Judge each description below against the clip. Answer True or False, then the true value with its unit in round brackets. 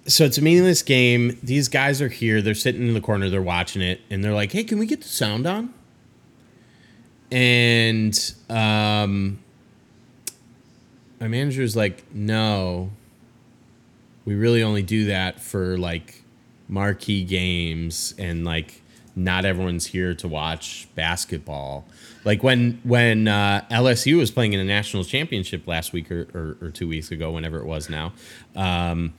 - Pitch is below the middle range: True (105 Hz)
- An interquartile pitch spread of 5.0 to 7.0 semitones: True (5.3 semitones)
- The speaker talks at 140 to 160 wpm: True (155 wpm)